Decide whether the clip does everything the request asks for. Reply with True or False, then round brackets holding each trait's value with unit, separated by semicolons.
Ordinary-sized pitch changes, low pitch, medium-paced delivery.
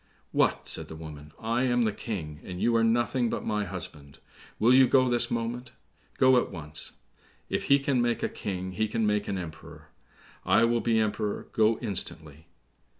False (5.9 semitones; 110 Hz; 185 wpm)